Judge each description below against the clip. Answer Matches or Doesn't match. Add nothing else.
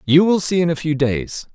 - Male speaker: Matches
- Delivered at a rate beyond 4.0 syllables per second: Matches